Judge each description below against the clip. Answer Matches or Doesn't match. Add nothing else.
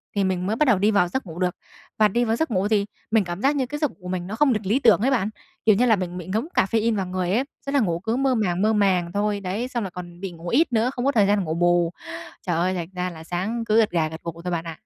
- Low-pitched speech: Doesn't match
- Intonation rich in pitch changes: Doesn't match